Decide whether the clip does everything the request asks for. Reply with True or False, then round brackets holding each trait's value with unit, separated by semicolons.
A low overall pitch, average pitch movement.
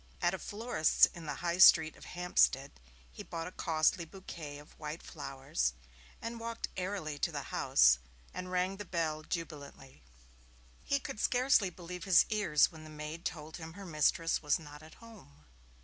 False (165 Hz; 3.5 semitones)